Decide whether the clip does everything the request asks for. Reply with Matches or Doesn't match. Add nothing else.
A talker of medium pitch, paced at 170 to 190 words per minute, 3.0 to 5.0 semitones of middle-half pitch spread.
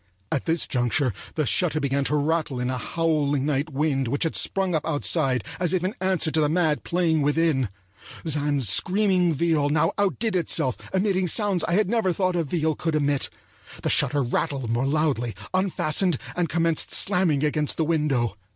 Matches